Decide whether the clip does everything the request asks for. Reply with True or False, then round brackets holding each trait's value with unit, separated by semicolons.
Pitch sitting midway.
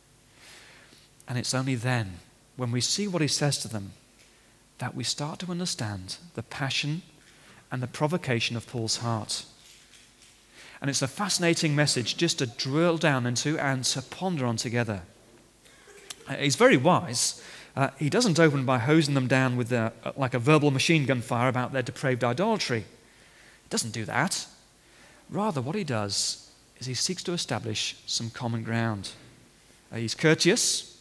False (130 Hz)